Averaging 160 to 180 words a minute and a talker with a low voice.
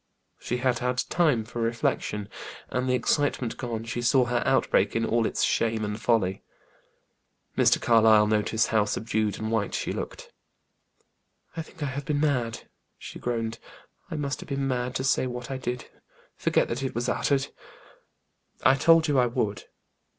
Yes: average, 170 wpm; low, 120 Hz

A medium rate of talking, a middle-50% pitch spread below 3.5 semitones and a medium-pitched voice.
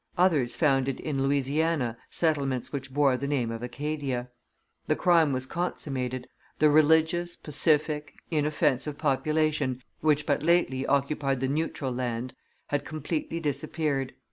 No: slow, 125 wpm; average, 2.9 semitones; medium, 145 Hz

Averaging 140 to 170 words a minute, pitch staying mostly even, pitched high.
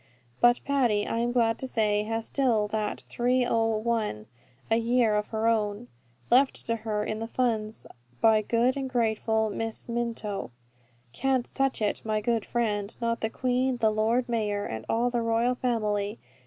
Yes: average, 165 wpm; narrow, 2.1 semitones; high, 225 Hz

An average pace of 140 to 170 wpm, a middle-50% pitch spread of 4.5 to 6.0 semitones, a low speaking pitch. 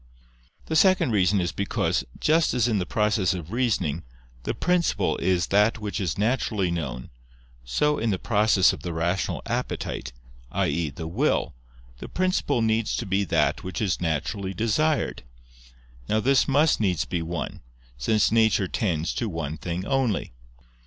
Yes: average, 155 wpm; average, 5.1 semitones; low, 100 Hz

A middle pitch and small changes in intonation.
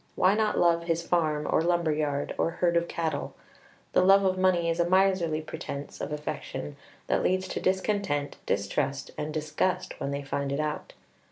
No: medium, 165 Hz; average, 3.6 semitones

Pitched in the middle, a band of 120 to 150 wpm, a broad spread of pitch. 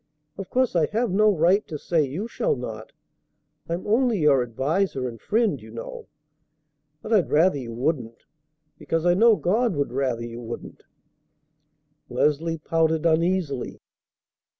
Yes: medium, 165 Hz; average, 145 wpm; wide, 6.5 semitones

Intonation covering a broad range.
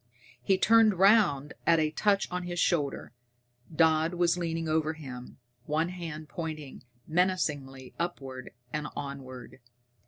No: average, 3.6 semitones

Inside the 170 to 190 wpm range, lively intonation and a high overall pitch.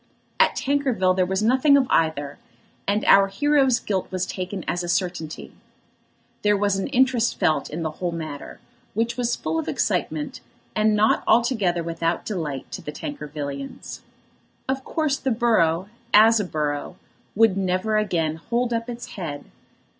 No: average, 155 wpm; wide, 6.1 semitones; high, 195 Hz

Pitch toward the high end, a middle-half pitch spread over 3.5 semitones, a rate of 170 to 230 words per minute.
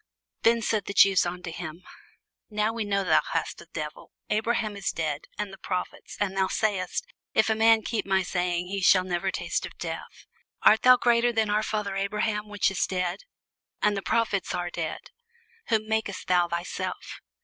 No: high, 200 Hz; average, 3.2 semitones; average, 185 wpm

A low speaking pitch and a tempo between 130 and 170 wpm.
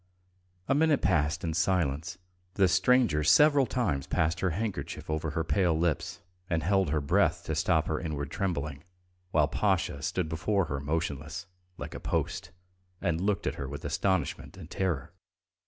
Yes: very low, 85 Hz; average, 160 wpm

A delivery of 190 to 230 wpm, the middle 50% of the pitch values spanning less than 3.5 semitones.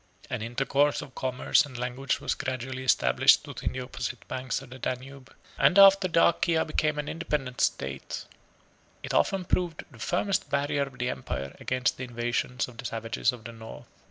No: average, 175 wpm; average, 3.1 semitones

